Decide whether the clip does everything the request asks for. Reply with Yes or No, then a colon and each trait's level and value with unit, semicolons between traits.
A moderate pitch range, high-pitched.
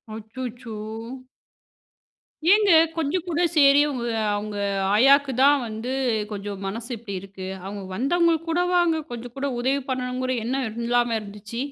Yes: average, 4.4 semitones; very high, 250 Hz